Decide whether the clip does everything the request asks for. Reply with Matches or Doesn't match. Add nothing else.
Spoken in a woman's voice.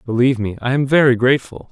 Doesn't match